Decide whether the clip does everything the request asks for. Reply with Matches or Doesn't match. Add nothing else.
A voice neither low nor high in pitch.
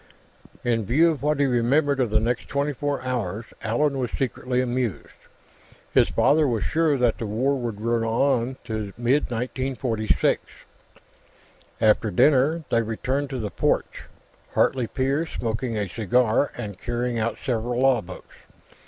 Doesn't match